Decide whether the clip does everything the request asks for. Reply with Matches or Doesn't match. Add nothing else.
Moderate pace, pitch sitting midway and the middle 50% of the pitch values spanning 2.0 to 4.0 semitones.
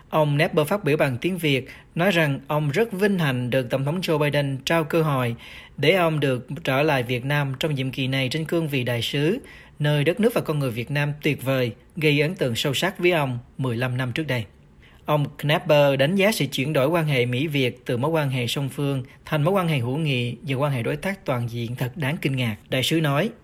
Matches